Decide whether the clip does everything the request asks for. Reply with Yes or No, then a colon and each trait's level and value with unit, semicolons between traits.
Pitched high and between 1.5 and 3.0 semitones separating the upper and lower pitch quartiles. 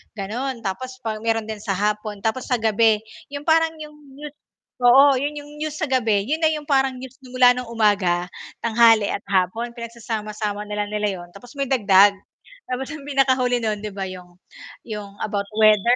No: high, 230 Hz; average, 4.1 semitones